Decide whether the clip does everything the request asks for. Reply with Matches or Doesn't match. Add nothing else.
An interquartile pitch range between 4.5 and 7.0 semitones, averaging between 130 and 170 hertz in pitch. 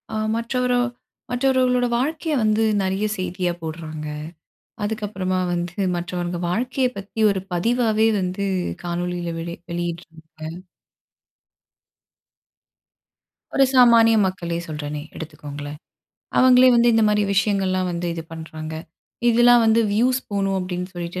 Doesn't match